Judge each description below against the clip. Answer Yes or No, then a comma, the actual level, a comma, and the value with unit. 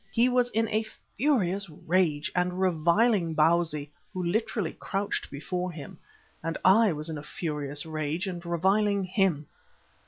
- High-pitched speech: No, medium, 180 Hz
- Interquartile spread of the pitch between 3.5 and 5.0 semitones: Yes, average, 4.3 semitones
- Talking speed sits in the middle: Yes, average, 145 wpm